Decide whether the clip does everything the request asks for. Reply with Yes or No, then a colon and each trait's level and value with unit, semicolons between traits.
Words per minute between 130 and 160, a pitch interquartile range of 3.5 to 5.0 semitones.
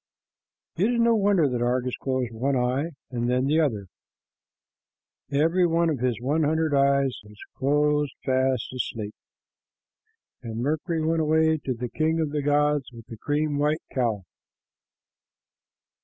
Yes: average, 140 wpm; average, 4.0 semitones